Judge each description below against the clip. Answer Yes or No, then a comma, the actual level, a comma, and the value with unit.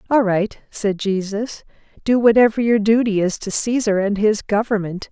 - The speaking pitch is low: No, high, 210 Hz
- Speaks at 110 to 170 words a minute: Yes, average, 165 wpm